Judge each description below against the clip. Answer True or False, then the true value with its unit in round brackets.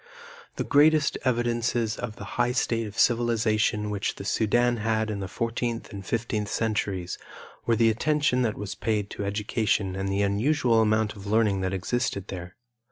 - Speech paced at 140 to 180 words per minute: True (165 wpm)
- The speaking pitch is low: True (110 Hz)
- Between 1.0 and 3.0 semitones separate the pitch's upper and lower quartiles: True (2.7 semitones)